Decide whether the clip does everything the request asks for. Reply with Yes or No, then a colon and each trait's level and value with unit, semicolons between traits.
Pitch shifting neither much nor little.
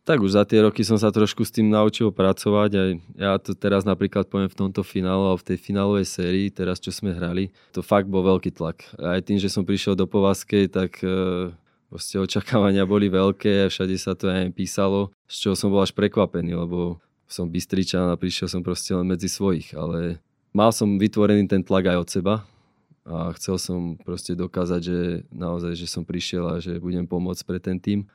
No: narrow, 1.9 semitones